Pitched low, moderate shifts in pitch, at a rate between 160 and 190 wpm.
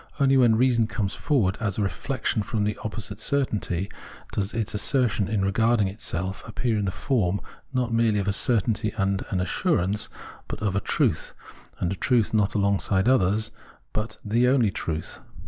Yes: low, 105 Hz; average, 3.0 semitones; average, 170 wpm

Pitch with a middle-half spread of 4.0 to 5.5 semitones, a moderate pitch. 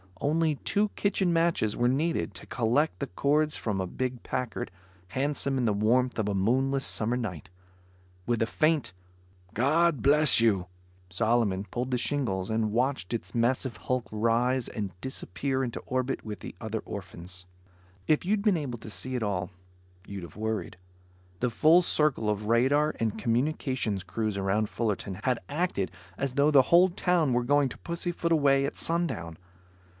No: average, 5.2 semitones; low, 125 Hz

